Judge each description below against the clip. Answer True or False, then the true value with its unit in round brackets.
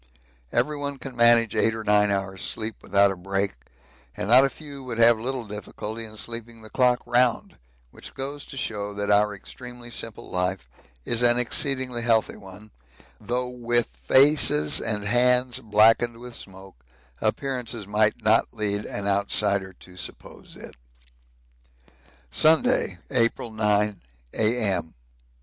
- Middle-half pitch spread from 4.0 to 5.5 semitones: False (3.2 semitones)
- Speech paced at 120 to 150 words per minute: True (140 wpm)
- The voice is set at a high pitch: False (115 Hz)